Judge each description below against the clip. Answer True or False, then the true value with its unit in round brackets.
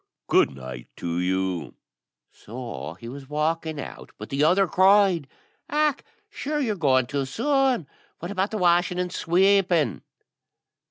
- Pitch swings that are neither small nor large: False (7.4 semitones)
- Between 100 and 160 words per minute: True (140 wpm)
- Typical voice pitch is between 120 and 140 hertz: False (165 Hz)